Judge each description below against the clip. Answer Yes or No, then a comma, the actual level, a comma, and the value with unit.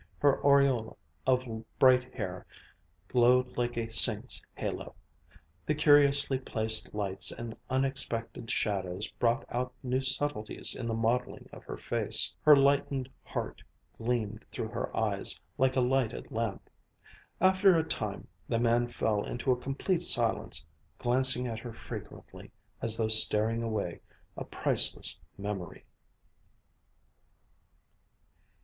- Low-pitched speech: Yes, low, 120 Hz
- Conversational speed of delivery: No, slow, 125 wpm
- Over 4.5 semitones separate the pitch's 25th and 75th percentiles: No, average, 3.1 semitones